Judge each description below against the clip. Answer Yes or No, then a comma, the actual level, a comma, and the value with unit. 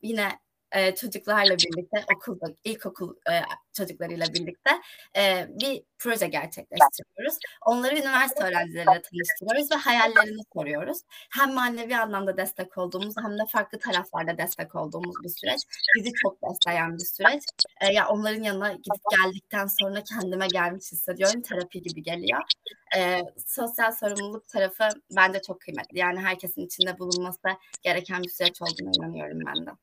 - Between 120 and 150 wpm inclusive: Yes, fast, 140 wpm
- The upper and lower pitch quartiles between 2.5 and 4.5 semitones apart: Yes, average, 3.8 semitones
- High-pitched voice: Yes, high, 195 Hz